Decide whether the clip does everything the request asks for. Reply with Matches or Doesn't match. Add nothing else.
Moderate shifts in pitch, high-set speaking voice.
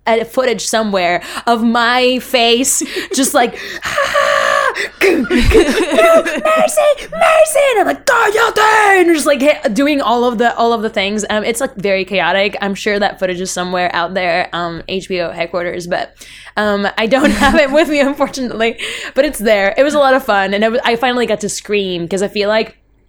Doesn't match